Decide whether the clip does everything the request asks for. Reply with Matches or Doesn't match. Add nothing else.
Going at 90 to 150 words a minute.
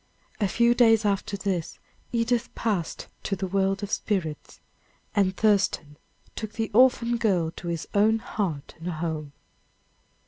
Matches